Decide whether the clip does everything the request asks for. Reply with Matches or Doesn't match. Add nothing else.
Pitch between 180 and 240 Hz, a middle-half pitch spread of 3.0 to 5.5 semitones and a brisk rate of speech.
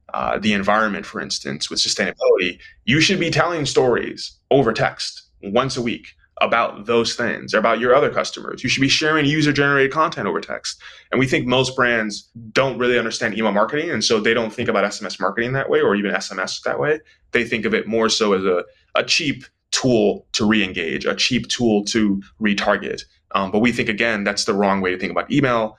Doesn't match